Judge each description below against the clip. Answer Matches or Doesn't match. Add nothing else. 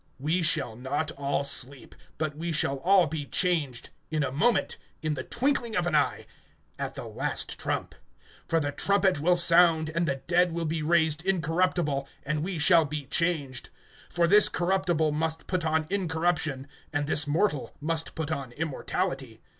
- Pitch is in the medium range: Matches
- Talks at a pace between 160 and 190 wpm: Matches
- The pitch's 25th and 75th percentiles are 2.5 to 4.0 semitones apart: Matches